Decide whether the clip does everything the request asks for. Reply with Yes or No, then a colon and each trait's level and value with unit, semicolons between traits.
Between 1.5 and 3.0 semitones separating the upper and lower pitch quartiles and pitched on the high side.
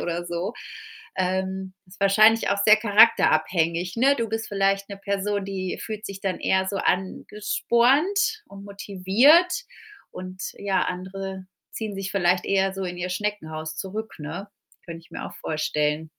Yes: narrow, 2.5 semitones; high, 195 Hz